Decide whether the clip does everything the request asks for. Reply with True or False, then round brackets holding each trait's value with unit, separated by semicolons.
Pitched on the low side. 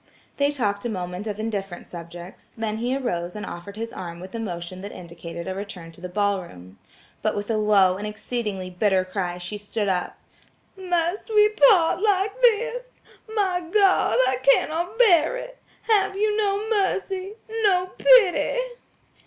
False (220 Hz)